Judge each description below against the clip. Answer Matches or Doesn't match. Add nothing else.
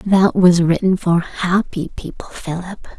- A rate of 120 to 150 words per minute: Matches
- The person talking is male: Doesn't match